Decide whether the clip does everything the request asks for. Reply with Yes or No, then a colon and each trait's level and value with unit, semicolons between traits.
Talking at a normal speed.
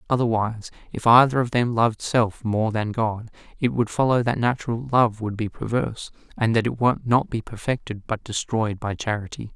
Yes: average, 190 wpm